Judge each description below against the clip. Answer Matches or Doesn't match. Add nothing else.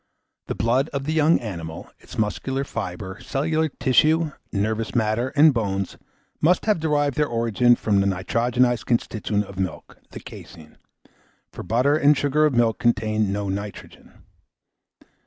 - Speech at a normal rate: Matches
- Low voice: Matches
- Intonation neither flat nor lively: Doesn't match